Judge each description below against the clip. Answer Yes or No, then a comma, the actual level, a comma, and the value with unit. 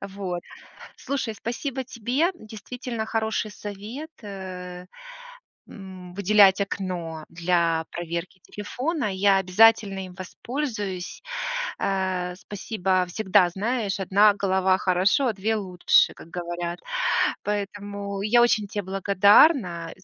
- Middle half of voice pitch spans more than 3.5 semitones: No, average, 3.1 semitones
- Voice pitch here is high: Yes, high, 195 Hz